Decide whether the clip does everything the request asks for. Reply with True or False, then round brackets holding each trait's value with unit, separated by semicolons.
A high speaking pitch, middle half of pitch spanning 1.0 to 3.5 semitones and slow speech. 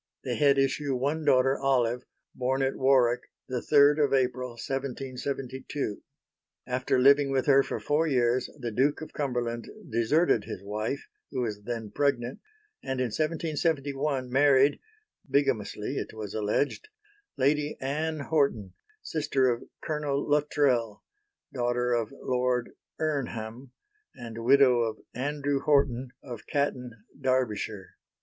False (130 Hz; 2.9 semitones; 120 wpm)